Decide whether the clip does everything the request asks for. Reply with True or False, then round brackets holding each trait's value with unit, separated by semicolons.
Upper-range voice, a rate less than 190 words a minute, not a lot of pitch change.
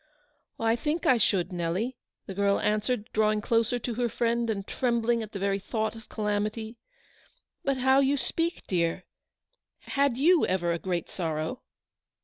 False (220 Hz; 165 wpm; 3.8 semitones)